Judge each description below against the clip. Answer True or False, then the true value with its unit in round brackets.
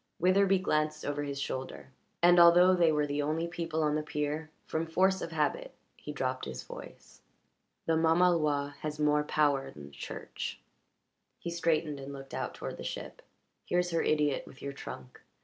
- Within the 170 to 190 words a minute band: True (175 wpm)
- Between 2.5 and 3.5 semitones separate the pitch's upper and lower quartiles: True (2.8 semitones)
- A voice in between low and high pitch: True (155 Hz)